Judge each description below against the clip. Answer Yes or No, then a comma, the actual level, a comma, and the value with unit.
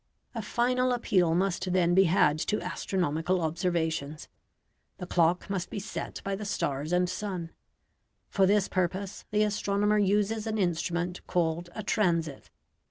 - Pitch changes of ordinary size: Yes, average, 3.3 semitones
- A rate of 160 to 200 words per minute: No, average, 145 wpm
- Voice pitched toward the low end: No, medium, 185 Hz